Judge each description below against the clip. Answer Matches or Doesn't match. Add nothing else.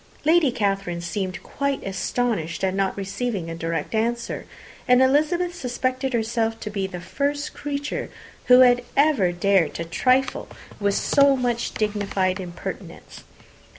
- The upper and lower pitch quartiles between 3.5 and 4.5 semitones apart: Doesn't match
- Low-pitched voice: Doesn't match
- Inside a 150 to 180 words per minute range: Doesn't match